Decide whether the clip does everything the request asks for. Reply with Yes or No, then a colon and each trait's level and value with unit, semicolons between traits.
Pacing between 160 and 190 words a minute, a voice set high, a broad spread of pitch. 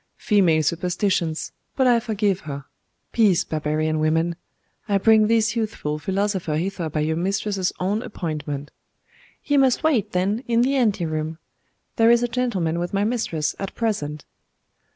No: average, 150 wpm; high, 195 Hz; wide, 5.9 semitones